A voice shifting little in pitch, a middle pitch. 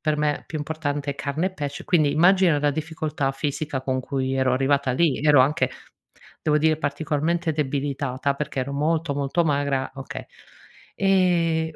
Yes: narrow, 2.3 semitones; medium, 145 Hz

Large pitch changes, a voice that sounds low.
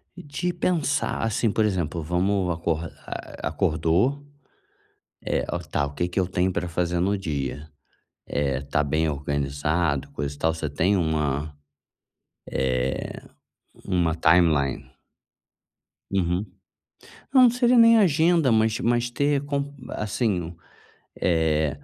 Yes: wide, 6.9 semitones; very low, 85 Hz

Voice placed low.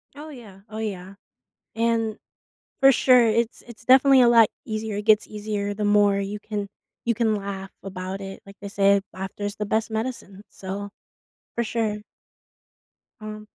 No: high, 210 Hz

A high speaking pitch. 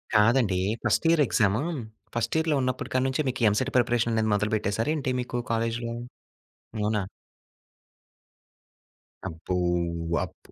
No: low, 115 Hz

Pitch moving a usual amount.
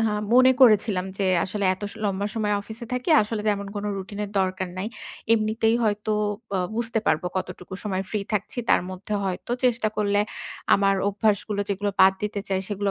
No: narrow, 1.9 semitones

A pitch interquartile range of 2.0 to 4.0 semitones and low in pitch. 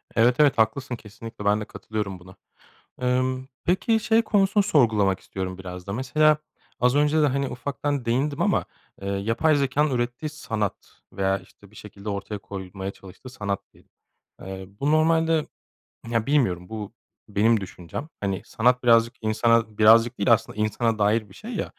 No: wide, 5.5 semitones; low, 115 Hz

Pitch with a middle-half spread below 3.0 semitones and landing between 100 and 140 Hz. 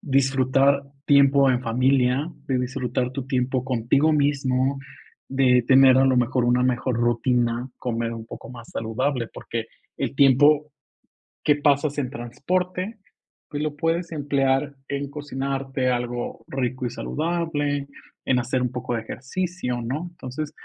Yes: narrow, 2.5 semitones; low, 135 Hz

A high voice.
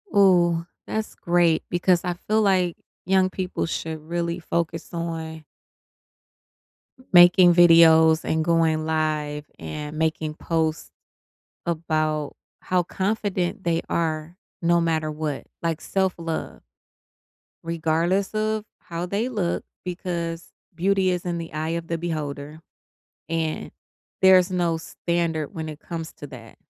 No: medium, 170 Hz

